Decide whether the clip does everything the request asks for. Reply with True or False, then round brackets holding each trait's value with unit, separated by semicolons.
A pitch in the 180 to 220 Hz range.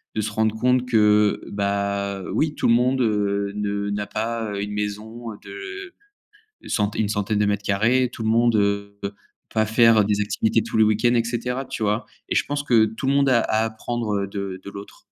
False (110 Hz)